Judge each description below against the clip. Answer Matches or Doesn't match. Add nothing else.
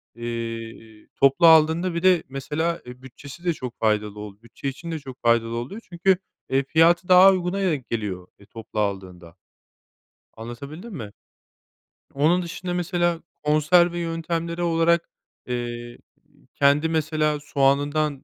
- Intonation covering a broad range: Matches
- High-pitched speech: Doesn't match